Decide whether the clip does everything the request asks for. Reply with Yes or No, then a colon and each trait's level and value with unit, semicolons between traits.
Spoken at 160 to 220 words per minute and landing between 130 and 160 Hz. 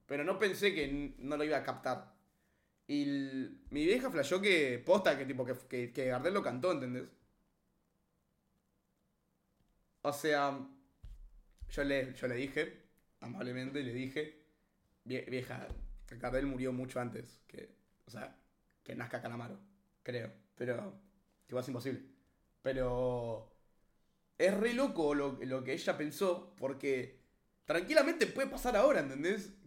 No: average, 135 wpm; medium, 140 Hz